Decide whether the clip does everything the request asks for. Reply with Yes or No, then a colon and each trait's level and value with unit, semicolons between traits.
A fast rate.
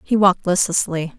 No: average, 150 wpm